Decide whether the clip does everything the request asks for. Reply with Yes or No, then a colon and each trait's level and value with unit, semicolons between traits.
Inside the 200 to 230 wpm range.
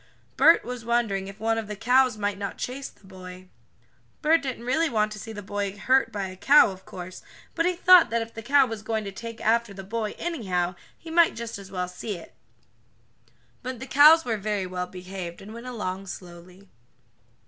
Yes: fast, 205 wpm